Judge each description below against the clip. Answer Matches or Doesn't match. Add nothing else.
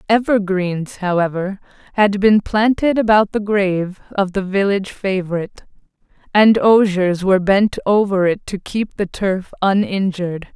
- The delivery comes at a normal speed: Doesn't match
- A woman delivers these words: Matches